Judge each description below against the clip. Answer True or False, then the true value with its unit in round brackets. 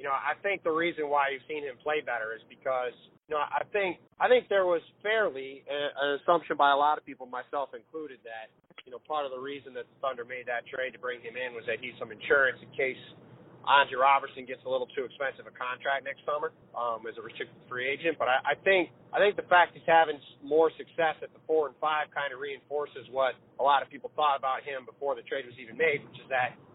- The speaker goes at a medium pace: False (245 wpm)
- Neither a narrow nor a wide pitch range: False (7.0 semitones)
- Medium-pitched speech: True (155 Hz)